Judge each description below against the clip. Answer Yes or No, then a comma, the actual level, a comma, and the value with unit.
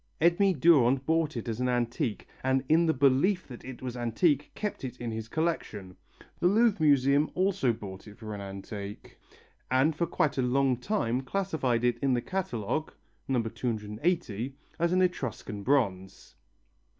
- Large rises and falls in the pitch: Yes, wide, 5.7 semitones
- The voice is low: Yes, low, 130 Hz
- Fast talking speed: No, average, 160 wpm